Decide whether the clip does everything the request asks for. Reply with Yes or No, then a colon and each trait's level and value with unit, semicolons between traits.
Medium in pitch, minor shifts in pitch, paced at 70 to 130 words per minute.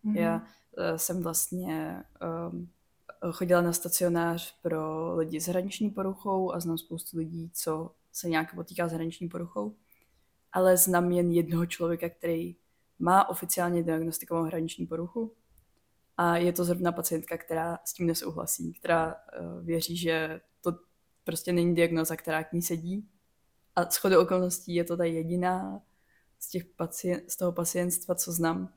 No: medium, 170 Hz; narrow, 1.5 semitones; average, 145 wpm